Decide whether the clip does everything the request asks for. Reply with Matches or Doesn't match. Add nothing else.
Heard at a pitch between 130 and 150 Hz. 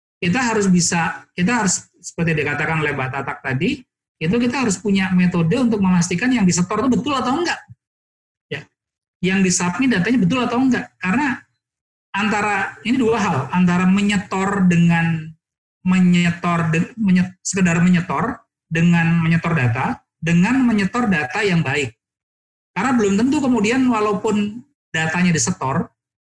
Doesn't match